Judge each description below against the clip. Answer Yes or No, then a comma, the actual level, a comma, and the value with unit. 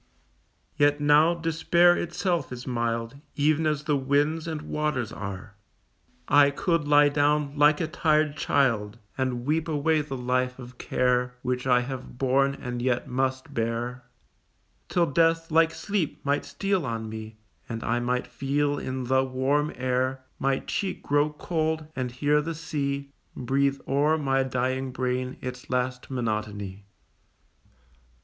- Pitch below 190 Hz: Yes, low, 135 Hz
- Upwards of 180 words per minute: No, average, 145 wpm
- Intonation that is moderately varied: Yes, average, 3.1 semitones